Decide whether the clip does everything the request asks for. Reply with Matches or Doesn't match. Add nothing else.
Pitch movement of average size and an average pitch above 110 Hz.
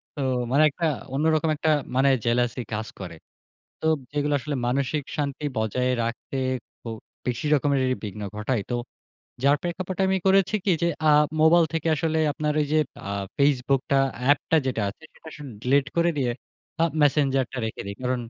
Matches